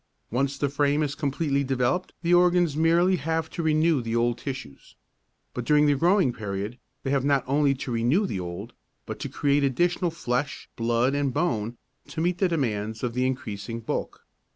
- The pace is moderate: Yes, average, 180 wpm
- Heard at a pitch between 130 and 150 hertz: Yes, medium, 140 Hz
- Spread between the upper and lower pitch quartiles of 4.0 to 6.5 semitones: Yes, average, 5.0 semitones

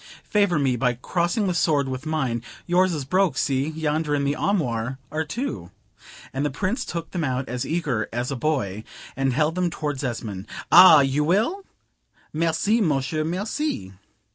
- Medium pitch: Yes, medium, 150 Hz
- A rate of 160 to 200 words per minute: Yes, average, 165 wpm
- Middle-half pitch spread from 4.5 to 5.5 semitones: Yes, average, 5.0 semitones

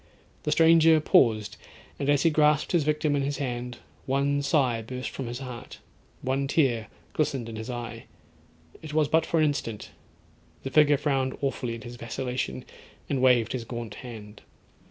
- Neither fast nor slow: Yes, average, 165 wpm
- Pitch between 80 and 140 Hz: Yes, low, 135 Hz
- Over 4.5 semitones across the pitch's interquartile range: No, average, 3.7 semitones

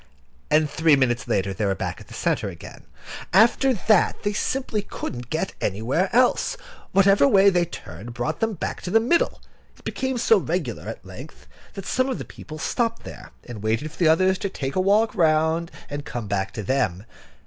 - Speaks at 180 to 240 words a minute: Yes, average, 195 wpm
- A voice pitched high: No, medium, 165 Hz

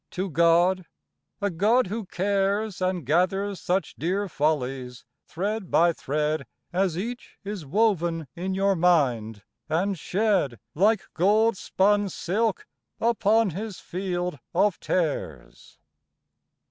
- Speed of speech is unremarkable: No, slow, 115 wpm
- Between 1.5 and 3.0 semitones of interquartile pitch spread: No, average, 3.6 semitones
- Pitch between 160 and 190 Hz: Yes, medium, 185 Hz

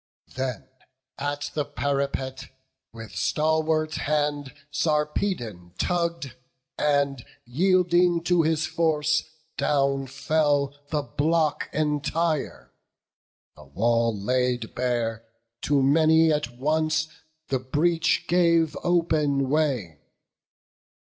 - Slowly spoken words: Yes, slow, 90 wpm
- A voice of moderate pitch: Yes, medium, 145 Hz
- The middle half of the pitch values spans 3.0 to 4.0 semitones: Yes, average, 3.3 semitones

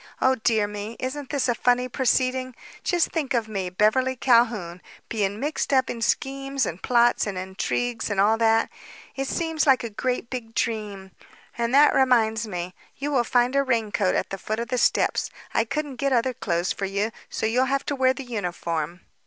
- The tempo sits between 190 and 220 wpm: Yes, average, 195 wpm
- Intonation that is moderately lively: Yes, average, 3.8 semitones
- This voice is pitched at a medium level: No, high, 235 Hz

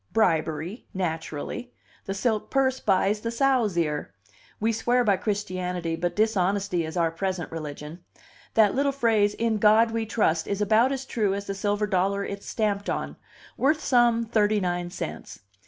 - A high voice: Yes, high, 205 Hz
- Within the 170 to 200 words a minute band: No, average, 160 wpm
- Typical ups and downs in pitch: Yes, average, 4.0 semitones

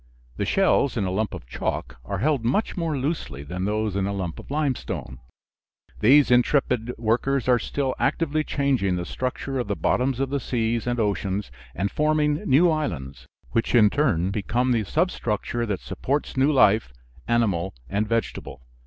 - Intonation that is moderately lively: No, wide, 5.7 semitones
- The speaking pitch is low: Yes, low, 120 Hz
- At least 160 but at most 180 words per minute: Yes, average, 165 wpm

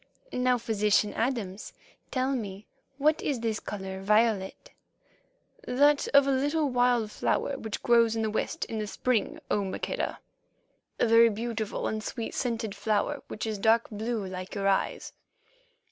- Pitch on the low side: No, high, 225 Hz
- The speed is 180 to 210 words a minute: No, average, 155 wpm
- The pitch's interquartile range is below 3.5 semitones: Yes, average, 3.0 semitones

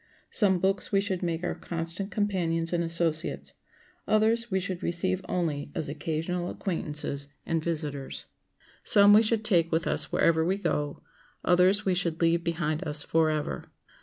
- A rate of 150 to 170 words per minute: Yes, average, 155 wpm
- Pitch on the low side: No, medium, 170 Hz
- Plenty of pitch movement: No, average, 3.0 semitones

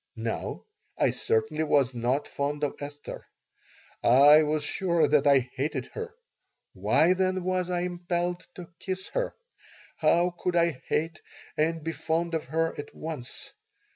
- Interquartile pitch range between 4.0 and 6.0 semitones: No, average, 3.3 semitones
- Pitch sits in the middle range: Yes, medium, 160 Hz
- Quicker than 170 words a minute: No, average, 145 wpm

